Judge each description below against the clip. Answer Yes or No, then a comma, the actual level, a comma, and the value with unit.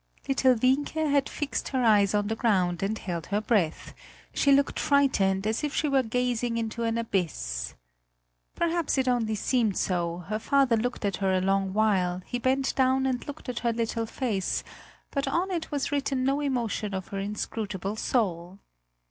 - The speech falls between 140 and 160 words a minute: No, average, 180 wpm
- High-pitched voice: Yes, high, 230 Hz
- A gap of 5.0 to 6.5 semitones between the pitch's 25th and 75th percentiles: Yes, average, 5.3 semitones